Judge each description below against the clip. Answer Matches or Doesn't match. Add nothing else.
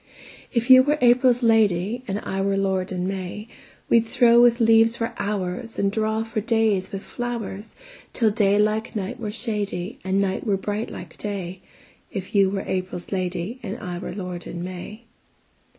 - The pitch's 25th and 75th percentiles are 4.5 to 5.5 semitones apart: Doesn't match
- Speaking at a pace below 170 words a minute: Matches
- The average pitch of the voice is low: Doesn't match